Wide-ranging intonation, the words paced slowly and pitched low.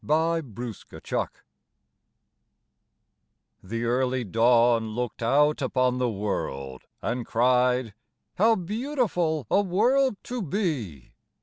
Yes: wide, 7.2 semitones; slow, 105 wpm; low, 125 Hz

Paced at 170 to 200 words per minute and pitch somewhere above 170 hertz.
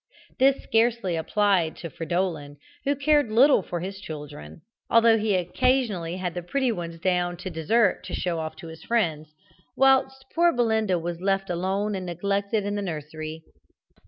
No: average, 160 wpm; high, 190 Hz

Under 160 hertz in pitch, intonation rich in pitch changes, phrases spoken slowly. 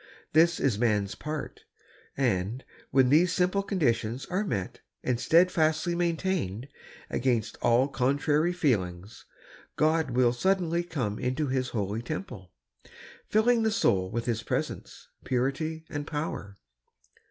Yes: low, 135 Hz; wide, 6.3 semitones; slow, 120 wpm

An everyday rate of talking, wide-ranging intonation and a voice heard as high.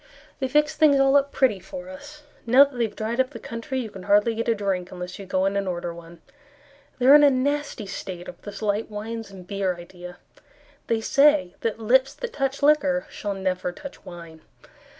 No: fast, 210 wpm; wide, 6.3 semitones; high, 225 Hz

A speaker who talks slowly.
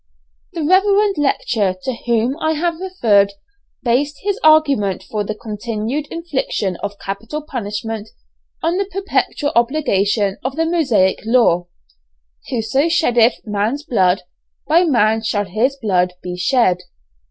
Yes: slow, 130 wpm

